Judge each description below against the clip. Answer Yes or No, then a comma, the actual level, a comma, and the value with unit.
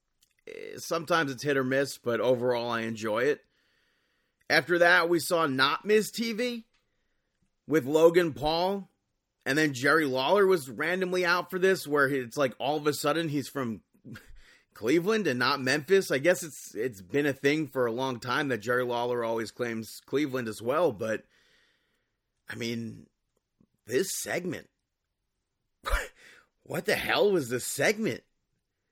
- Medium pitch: Yes, medium, 145 Hz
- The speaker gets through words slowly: No, average, 150 wpm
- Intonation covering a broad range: Yes, wide, 6.3 semitones